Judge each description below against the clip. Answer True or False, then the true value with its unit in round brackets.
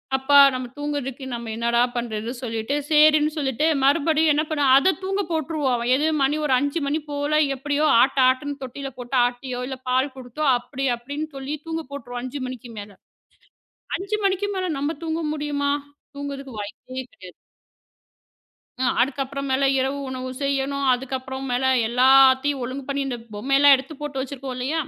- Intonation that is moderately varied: False (2.2 semitones)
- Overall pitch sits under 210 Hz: False (275 Hz)